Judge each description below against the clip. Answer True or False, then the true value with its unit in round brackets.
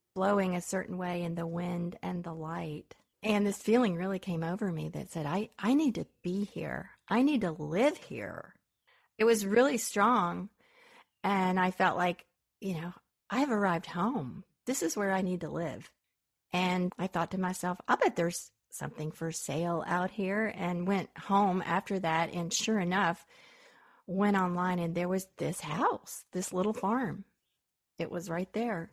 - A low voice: False (185 Hz)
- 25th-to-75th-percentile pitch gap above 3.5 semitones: False (3.2 semitones)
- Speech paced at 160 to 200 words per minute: True (175 wpm)